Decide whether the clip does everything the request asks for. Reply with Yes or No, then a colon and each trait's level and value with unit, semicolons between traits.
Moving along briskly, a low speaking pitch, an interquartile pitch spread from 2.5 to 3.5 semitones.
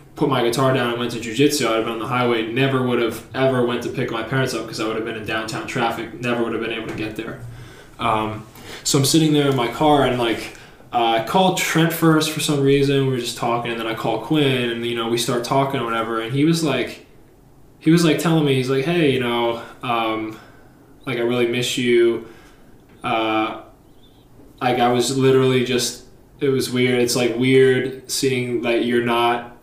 Yes: fast, 225 wpm; low, 120 Hz; average, 2.8 semitones